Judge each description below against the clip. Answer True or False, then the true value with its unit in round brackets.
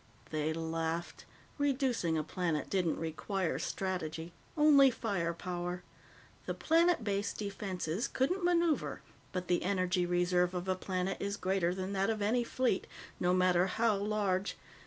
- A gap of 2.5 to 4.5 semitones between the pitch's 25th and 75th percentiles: True (3.5 semitones)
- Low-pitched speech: False (185 Hz)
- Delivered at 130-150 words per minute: True (140 wpm)